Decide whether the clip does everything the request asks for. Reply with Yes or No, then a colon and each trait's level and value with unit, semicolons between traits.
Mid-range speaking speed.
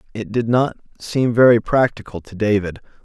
Yes: average, 160 wpm